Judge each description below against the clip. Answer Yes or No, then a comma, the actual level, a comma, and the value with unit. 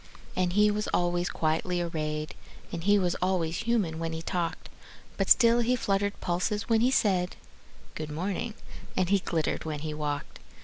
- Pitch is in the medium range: Yes, medium, 180 Hz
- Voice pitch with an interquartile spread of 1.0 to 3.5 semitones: No, average, 4.2 semitones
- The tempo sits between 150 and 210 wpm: Yes, average, 170 wpm